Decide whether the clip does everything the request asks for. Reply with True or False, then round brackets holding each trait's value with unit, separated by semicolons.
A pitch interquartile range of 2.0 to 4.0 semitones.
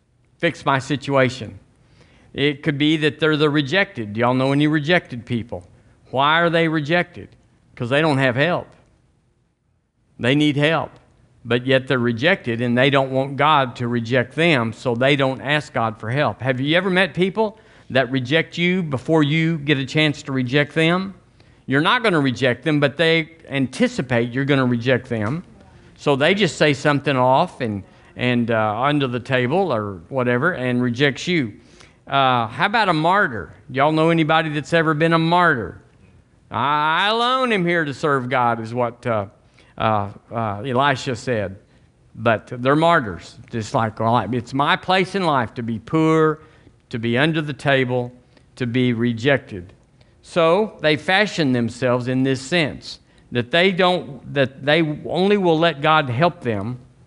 False (4.6 semitones)